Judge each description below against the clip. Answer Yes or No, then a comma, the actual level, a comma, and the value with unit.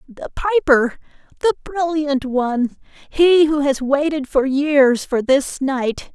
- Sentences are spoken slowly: Yes, slow, 115 wpm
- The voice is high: Yes, very high, 285 Hz